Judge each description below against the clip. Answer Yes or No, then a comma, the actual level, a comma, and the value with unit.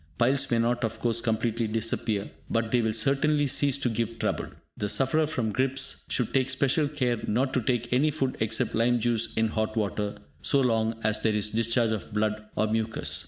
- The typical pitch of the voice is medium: No, low, 115 Hz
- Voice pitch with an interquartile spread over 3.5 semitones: No, average, 2.9 semitones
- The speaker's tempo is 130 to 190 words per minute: No, average, 200 wpm